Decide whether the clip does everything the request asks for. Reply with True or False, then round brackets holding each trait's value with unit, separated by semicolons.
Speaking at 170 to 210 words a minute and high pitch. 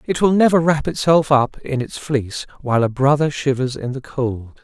False (205 wpm; 140 Hz)